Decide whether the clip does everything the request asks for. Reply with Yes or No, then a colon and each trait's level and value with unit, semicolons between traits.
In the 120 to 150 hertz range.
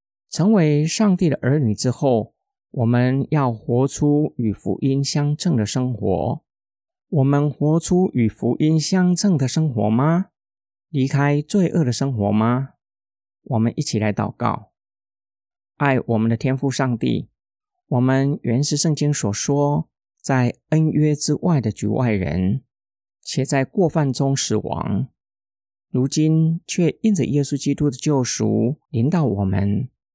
Yes: low, 135 Hz